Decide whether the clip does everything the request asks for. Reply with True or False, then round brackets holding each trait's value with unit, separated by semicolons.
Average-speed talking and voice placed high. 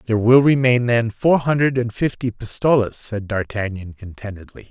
False (155 wpm; 115 Hz)